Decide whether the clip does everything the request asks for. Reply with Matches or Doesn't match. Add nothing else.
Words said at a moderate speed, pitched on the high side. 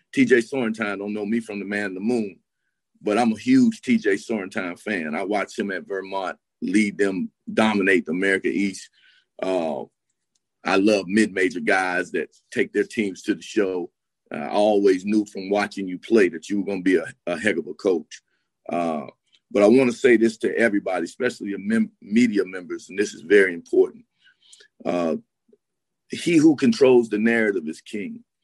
Doesn't match